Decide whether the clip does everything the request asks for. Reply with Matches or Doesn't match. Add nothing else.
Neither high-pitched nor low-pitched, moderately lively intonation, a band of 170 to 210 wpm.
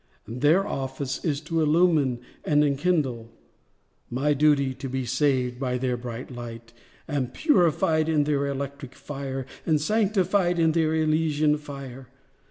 Doesn't match